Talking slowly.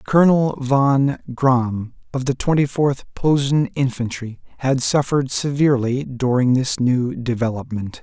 Yes: slow, 120 wpm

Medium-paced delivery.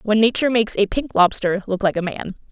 No: fast, 240 wpm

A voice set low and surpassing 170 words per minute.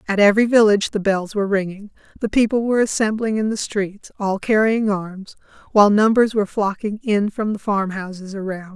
No: high, 205 Hz; average, 180 wpm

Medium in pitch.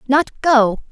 No: very high, 260 Hz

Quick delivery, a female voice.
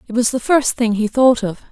Yes: fast, 280 wpm; female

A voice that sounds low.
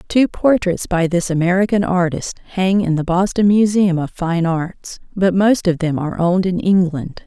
No: medium, 180 Hz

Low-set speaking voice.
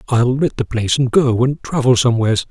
Yes: low, 120 Hz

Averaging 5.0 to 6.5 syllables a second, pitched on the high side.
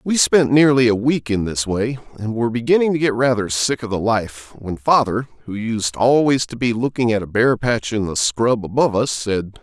No: 5.1 syllables/s; low, 120 Hz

